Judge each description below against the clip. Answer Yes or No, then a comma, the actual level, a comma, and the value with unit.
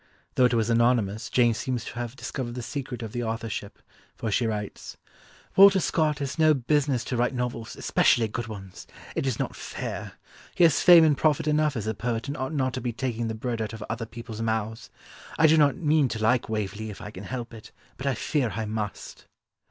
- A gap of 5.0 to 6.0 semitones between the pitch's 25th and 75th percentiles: No, average, 3.6 semitones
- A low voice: Yes, low, 120 Hz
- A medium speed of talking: No, fast, 215 wpm